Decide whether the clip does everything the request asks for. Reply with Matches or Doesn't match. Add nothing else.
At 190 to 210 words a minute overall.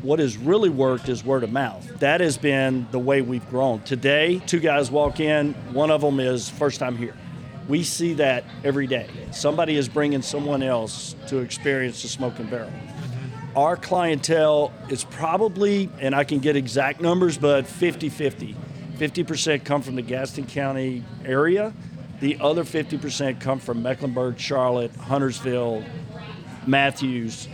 Doesn't match